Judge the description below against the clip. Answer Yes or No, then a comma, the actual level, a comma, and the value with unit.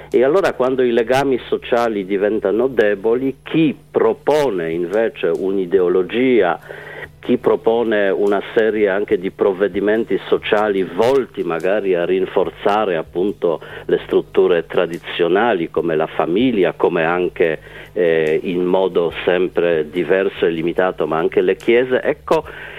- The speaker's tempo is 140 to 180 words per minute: No, average, 120 wpm